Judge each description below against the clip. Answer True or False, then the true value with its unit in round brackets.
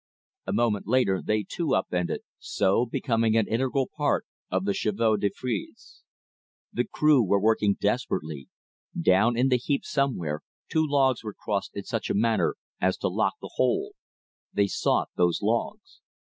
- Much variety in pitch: False (4.2 semitones)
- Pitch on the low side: True (110 Hz)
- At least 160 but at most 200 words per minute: True (165 wpm)